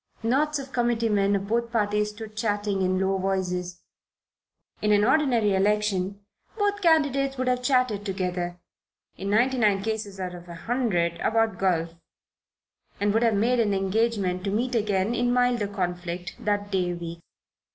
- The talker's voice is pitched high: Yes, high, 205 Hz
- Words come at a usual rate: Yes, average, 160 wpm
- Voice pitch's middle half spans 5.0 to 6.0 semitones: No, average, 3.9 semitones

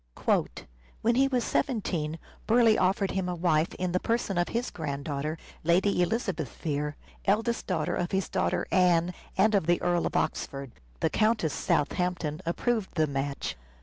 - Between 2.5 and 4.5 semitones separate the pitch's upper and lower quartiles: No, average, 5.0 semitones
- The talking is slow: No, average, 160 wpm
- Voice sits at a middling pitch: Yes, medium, 180 Hz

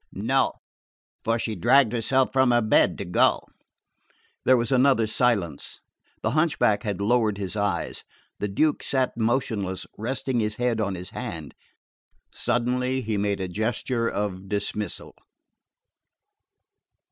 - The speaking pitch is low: Yes, low, 110 Hz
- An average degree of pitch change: Yes, average, 3.7 semitones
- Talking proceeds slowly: Yes, slow, 130 wpm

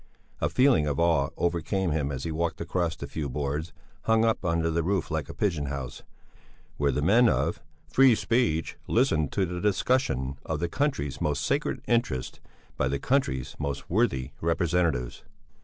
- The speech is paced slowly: No, average, 170 wpm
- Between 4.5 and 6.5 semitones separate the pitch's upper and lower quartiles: Yes, wide, 5.6 semitones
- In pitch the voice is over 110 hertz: No, very low, 80 Hz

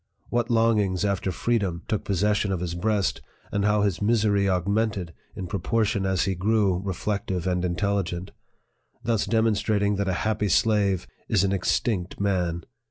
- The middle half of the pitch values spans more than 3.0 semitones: No, narrow, 2.4 semitones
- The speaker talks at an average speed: Yes, average, 150 wpm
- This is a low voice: Yes, low, 100 Hz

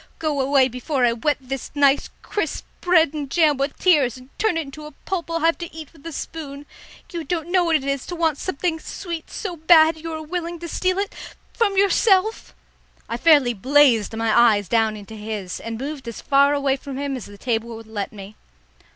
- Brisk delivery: Yes, fast, 210 wpm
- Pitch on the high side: Yes, very high, 290 Hz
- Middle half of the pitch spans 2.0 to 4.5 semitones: No, average, 5.2 semitones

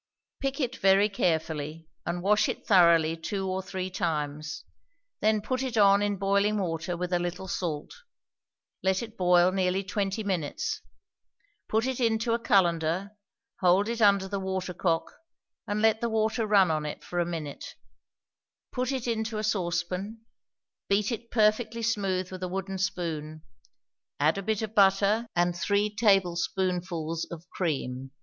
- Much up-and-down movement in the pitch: No, average, 3.5 semitones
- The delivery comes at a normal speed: Yes, average, 155 wpm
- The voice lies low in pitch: No, high, 190 Hz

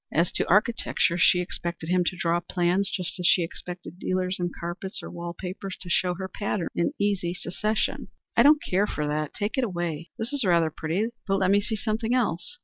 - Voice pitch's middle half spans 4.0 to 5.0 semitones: No, average, 2.9 semitones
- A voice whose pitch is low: No, medium, 180 Hz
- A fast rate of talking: Yes, fast, 210 wpm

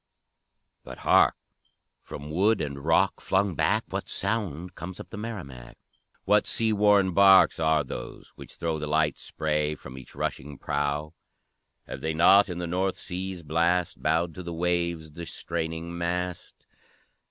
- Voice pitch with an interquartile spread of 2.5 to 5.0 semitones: Yes, average, 3.3 semitones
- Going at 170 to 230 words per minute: No, average, 155 wpm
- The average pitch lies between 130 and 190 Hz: No, very low, 85 Hz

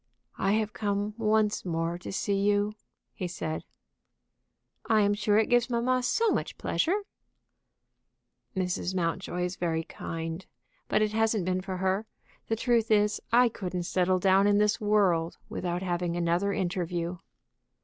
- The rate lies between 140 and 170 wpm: Yes, average, 150 wpm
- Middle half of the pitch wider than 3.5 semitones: No, average, 3.2 semitones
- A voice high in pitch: Yes, high, 195 Hz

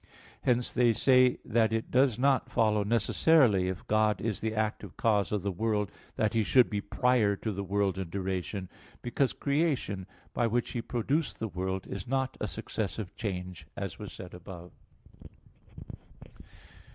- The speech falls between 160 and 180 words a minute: Yes, average, 165 wpm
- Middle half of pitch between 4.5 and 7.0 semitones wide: No, average, 3.9 semitones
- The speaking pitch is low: Yes, low, 110 Hz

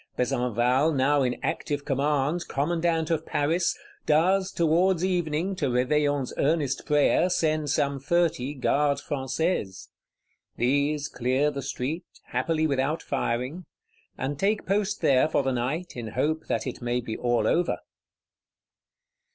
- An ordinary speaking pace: No, slow, 130 wpm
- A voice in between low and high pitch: Yes, medium, 145 Hz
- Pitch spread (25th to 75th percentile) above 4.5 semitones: No, average, 3.7 semitones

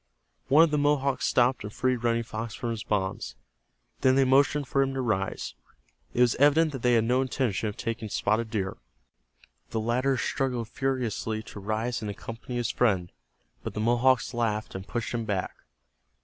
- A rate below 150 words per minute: No, average, 180 wpm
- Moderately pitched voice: No, low, 120 Hz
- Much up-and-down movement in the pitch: No, average, 3.3 semitones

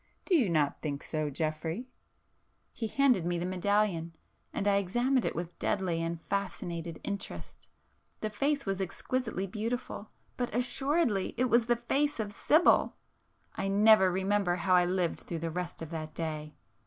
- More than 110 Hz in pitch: Yes, high, 190 Hz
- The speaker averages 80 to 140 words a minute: No, average, 150 wpm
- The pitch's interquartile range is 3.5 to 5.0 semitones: No, wide, 5.5 semitones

